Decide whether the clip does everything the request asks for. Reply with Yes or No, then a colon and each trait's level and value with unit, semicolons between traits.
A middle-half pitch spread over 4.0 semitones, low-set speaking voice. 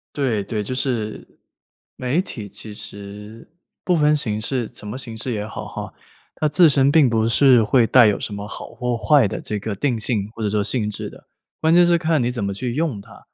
Yes: average, 4.6 semitones; low, 115 Hz